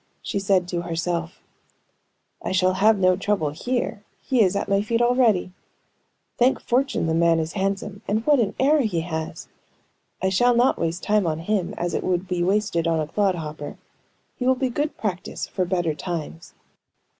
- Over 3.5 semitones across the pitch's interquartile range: Yes, average, 4.3 semitones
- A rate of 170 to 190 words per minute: Yes, average, 180 wpm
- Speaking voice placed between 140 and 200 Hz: Yes, high, 190 Hz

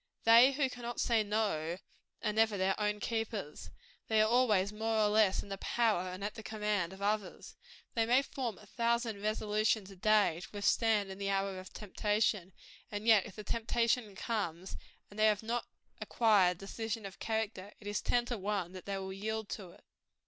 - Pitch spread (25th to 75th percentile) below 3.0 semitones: Yes, narrow, 2.4 semitones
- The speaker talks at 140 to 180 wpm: No, average, 190 wpm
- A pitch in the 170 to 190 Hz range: No, high, 210 Hz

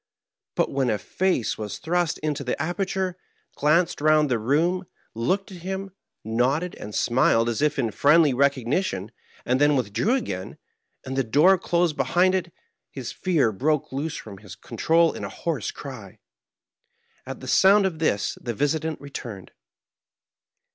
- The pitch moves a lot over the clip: Yes, wide, 6.5 semitones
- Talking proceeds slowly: No, average, 155 wpm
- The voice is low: No, medium, 145 Hz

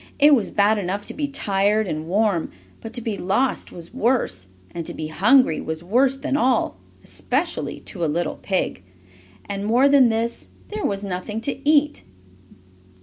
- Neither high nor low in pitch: No, high, 215 Hz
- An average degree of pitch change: No, wide, 6.2 semitones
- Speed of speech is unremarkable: Yes, average, 170 wpm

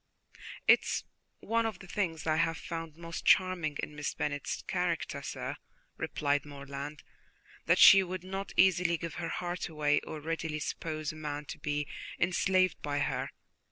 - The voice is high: No, medium, 165 Hz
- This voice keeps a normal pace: Yes, average, 160 wpm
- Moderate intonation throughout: Yes, average, 3.3 semitones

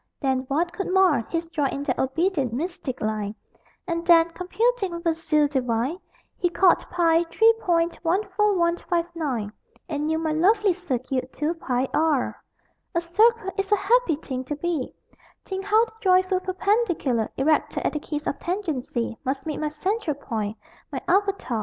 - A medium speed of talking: Yes, average, 160 wpm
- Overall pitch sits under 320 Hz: No, very high, 330 Hz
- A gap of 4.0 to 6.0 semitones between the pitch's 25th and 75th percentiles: Yes, average, 5.2 semitones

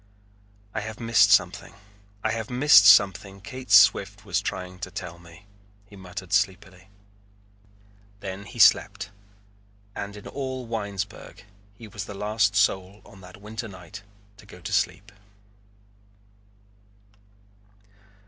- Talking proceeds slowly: Yes, slow, 125 wpm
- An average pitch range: No, narrow, 2.3 semitones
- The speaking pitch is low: Yes, low, 100 Hz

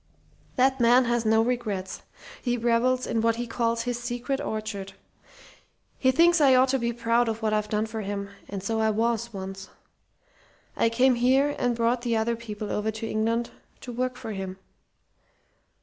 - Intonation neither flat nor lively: No, narrow, 2.1 semitones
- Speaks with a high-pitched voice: Yes, high, 230 Hz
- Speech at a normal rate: Yes, average, 180 wpm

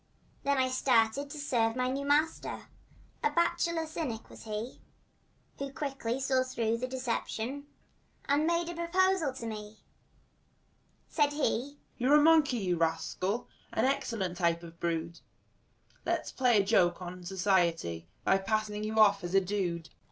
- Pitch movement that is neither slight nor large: No, wide, 6.6 semitones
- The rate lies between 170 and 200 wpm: No, average, 160 wpm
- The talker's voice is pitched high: Yes, high, 230 Hz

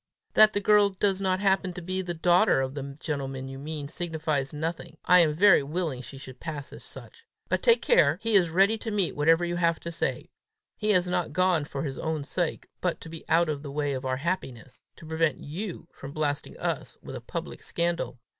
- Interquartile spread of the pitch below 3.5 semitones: No, average, 4.2 semitones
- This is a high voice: No, medium, 165 Hz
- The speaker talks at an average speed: No, fast, 220 wpm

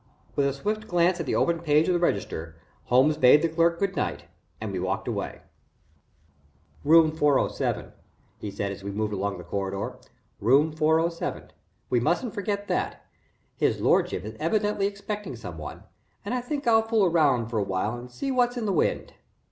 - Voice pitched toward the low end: No, medium, 155 Hz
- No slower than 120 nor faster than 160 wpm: No, average, 180 wpm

